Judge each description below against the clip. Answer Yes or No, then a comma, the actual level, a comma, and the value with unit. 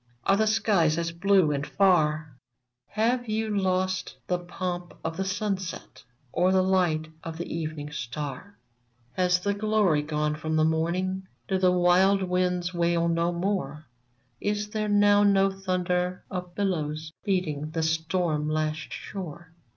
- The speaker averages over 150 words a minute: No, average, 145 wpm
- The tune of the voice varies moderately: Yes, average, 3.3 semitones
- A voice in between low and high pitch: Yes, medium, 180 Hz